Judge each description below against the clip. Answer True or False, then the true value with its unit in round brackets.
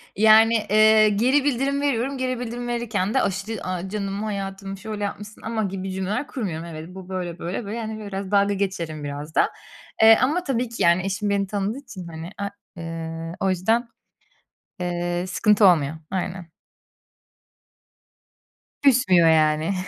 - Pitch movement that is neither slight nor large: True (3.9 semitones)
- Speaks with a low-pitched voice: False (200 Hz)